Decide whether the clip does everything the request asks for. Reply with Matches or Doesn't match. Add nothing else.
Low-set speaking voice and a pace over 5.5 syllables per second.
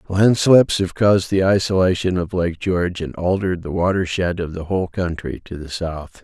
Doesn't match